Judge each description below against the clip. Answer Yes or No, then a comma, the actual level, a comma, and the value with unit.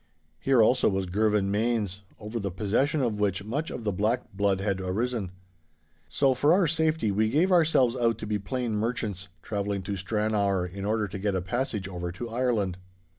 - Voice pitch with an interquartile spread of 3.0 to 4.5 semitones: Yes, average, 3.8 semitones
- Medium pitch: No, low, 105 Hz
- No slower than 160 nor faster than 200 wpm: Yes, average, 185 wpm